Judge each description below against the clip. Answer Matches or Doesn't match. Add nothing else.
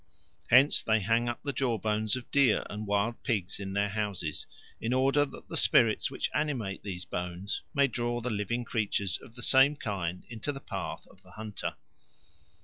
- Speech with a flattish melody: Doesn't match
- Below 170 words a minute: Doesn't match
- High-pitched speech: Doesn't match